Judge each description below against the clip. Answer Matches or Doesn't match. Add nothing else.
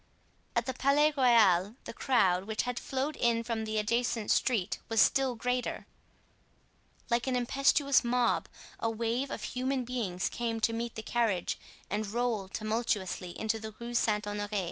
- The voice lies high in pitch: Matches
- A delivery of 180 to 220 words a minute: Doesn't match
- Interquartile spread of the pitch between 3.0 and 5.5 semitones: Doesn't match